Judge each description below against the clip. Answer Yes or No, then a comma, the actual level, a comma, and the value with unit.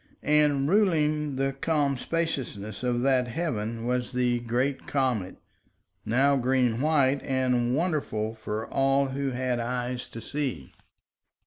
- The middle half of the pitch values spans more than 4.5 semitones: No, average, 2.8 semitones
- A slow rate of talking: Yes, slow, 125 wpm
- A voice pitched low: Yes, low, 130 Hz